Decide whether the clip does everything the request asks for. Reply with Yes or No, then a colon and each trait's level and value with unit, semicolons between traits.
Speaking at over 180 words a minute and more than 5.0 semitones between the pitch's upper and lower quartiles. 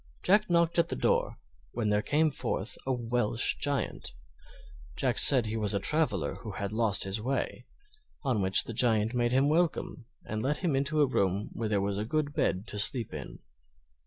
Yes: average, 190 wpm; wide, 5.4 semitones